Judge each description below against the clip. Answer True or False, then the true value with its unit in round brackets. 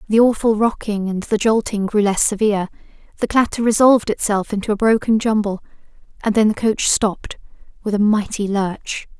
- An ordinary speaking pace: True (170 wpm)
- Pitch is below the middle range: False (210 Hz)